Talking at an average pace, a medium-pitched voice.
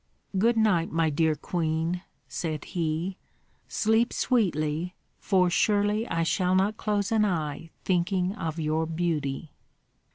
No: slow, 125 wpm; medium, 175 Hz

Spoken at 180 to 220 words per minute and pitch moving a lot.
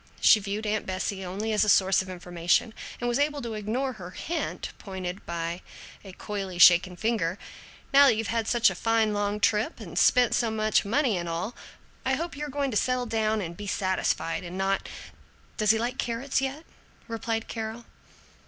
No: average, 190 wpm; average, 4.0 semitones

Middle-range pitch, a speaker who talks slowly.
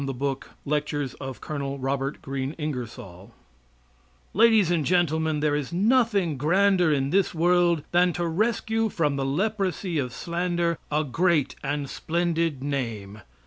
Yes: medium, 155 Hz; slow, 130 wpm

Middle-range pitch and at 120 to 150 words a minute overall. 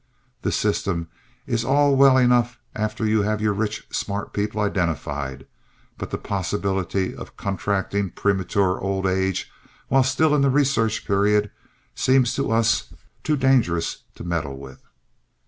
No: low, 105 Hz; average, 140 wpm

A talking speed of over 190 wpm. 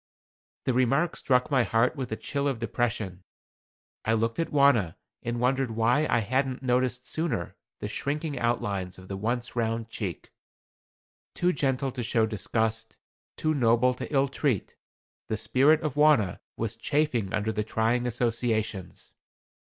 No: average, 150 wpm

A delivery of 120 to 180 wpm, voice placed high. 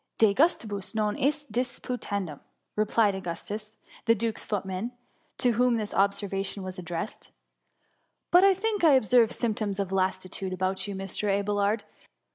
Yes: average, 150 wpm; high, 210 Hz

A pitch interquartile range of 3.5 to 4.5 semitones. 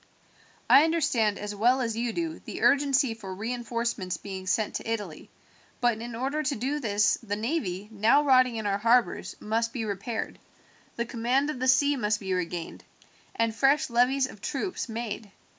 Yes: average, 4.1 semitones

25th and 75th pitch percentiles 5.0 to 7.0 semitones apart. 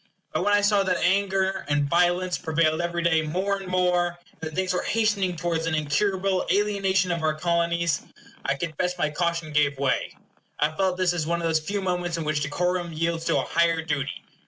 No: average, 2.7 semitones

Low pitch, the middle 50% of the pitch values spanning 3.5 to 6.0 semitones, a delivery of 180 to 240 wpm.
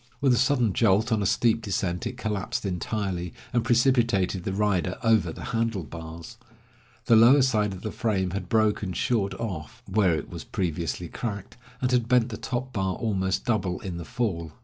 Yes: low, 105 Hz; average, 4.1 semitones; average, 185 wpm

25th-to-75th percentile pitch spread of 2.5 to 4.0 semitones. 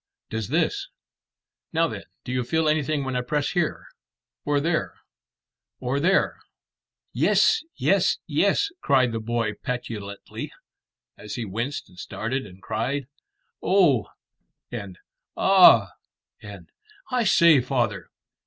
No: wide, 5.4 semitones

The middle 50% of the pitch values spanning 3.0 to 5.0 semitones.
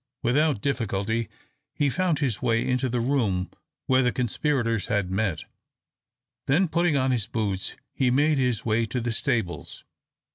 Yes: average, 3.8 semitones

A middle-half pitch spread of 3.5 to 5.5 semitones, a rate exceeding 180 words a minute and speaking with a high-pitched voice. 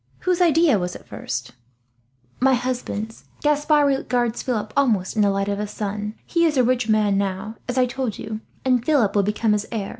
Yes: average, 4.2 semitones; average, 200 wpm; high, 225 Hz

